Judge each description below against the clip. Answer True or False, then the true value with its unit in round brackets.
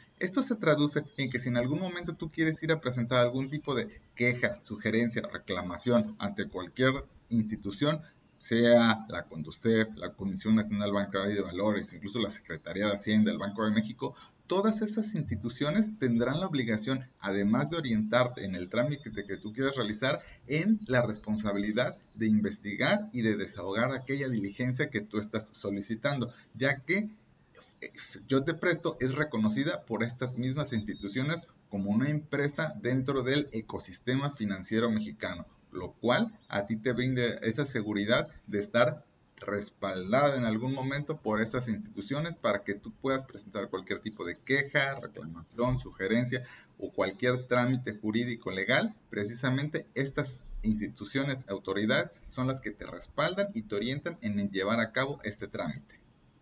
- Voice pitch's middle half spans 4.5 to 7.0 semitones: True (4.8 semitones)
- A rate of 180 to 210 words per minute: False (150 wpm)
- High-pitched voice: False (120 Hz)